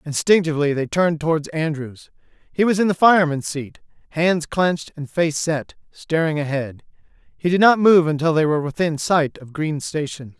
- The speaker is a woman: No, male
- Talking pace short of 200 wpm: Yes, average, 175 wpm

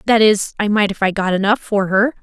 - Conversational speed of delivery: No, fast, 270 wpm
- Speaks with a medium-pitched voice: No, high, 205 Hz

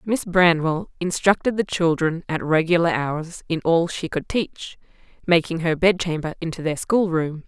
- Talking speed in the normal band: Yes, average, 160 wpm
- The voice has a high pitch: No, medium, 170 Hz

